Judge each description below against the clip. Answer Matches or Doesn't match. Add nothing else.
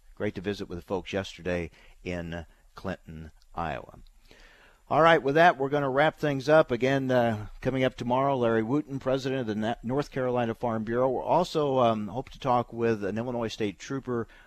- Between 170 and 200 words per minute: Matches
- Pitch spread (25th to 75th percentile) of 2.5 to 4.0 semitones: Doesn't match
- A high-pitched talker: Doesn't match